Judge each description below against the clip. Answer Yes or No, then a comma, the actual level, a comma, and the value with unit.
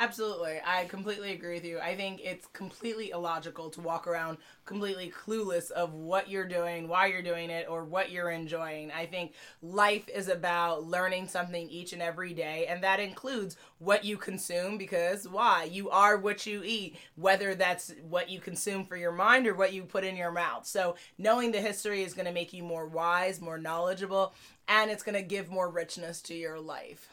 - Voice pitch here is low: No, medium, 180 Hz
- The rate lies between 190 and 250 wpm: Yes, average, 200 wpm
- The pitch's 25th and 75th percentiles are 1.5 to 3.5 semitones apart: Yes, narrow, 2.5 semitones